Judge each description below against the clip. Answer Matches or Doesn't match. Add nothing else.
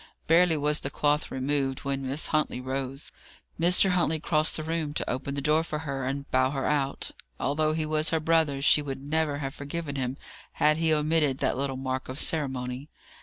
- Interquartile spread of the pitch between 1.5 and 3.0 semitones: Matches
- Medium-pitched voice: Matches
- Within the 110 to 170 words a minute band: Doesn't match